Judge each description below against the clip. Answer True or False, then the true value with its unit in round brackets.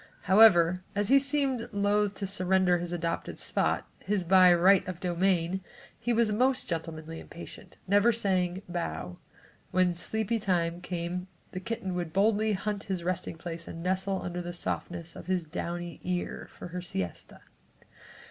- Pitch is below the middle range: False (185 Hz)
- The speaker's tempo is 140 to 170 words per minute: True (160 wpm)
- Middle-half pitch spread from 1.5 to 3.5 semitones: True (2.7 semitones)